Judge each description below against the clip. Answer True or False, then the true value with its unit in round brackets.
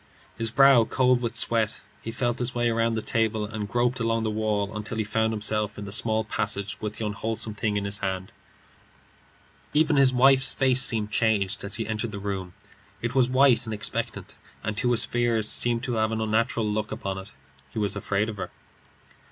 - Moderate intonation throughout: False (2.2 semitones)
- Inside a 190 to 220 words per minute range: True (200 wpm)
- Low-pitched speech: True (110 Hz)